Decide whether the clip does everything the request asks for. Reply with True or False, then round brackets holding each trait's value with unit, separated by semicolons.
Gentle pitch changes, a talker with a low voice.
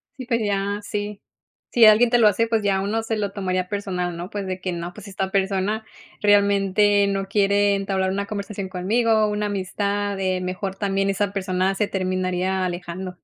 False (1.6 semitones; 200 Hz)